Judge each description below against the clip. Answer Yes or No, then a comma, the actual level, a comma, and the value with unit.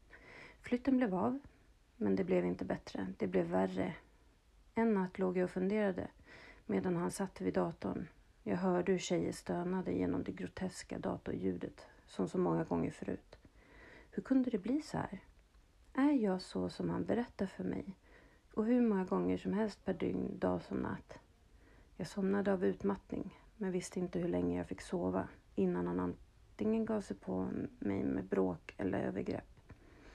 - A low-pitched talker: No, medium, 180 Hz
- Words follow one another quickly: No, average, 165 wpm